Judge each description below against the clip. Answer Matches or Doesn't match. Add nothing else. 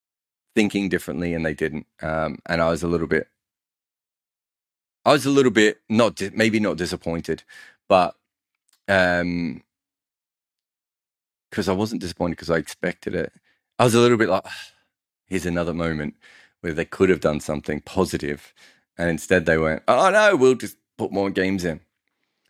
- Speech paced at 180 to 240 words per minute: Doesn't match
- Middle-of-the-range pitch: Doesn't match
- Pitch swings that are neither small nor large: Matches